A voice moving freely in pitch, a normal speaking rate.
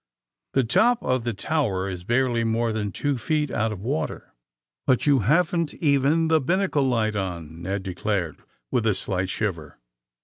Yes: wide, 6.8 semitones; average, 175 wpm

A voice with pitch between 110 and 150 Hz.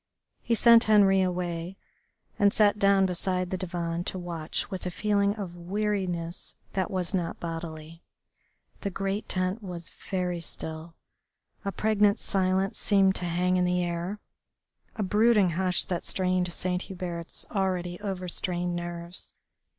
No: medium, 185 Hz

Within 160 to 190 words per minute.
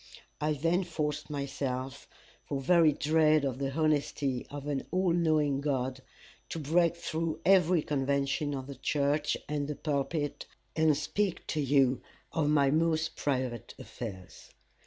No: average, 140 wpm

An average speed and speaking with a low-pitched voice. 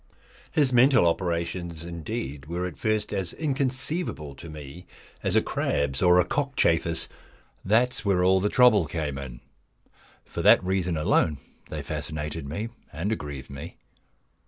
Yes: average, 145 wpm; very low, 85 Hz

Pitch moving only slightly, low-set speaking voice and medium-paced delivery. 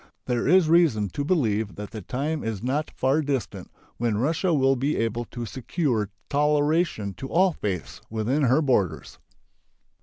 No: wide, 5.4 semitones; low, 130 Hz; average, 155 wpm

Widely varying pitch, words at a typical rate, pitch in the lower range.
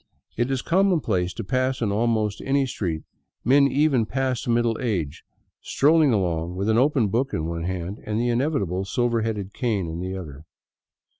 Yes: wide, 5.7 semitones; average, 170 wpm; low, 115 Hz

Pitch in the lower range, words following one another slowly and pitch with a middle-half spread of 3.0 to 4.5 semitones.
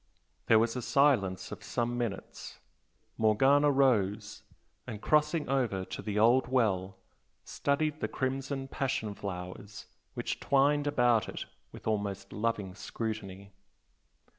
No: low, 115 Hz; slow, 120 wpm; average, 5.0 semitones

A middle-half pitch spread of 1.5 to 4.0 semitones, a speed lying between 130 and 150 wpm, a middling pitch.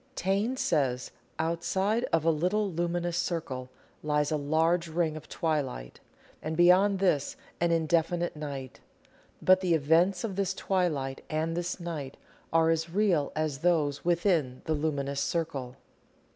Yes: average, 2.9 semitones; average, 140 wpm; medium, 165 Hz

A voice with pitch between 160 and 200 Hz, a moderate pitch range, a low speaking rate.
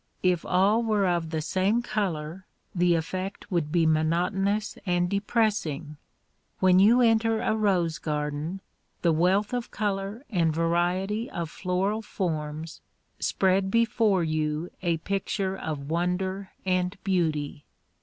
Yes: medium, 185 Hz; average, 3.5 semitones; slow, 125 wpm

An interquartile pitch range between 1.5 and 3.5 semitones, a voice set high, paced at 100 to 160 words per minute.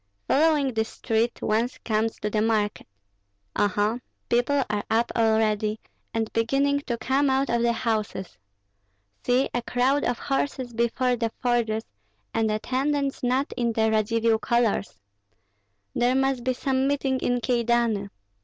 Yes: average, 2.9 semitones; high, 235 Hz; average, 140 wpm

